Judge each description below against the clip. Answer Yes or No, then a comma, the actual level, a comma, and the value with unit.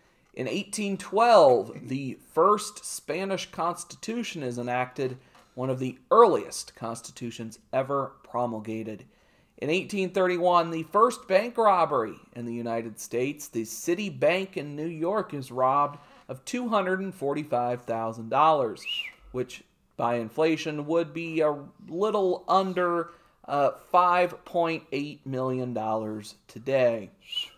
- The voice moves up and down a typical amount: No, wide, 6.4 semitones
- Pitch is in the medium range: Yes, medium, 145 Hz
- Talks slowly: Yes, slow, 100 wpm